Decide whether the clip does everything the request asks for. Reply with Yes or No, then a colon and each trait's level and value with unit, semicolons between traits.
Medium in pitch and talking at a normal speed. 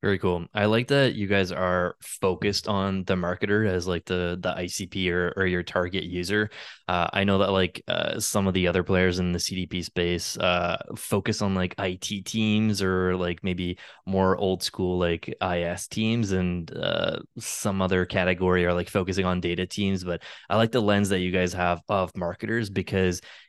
No: very low, 95 Hz; average, 190 wpm